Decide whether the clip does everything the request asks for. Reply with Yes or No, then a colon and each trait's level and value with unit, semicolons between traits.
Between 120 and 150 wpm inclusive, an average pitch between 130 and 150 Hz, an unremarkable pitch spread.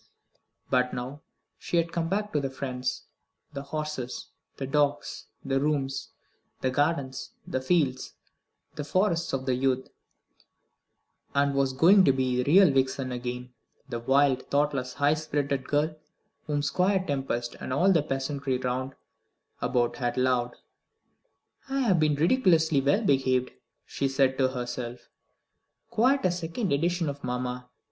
Yes: average, 140 wpm; medium, 140 Hz; average, 3.4 semitones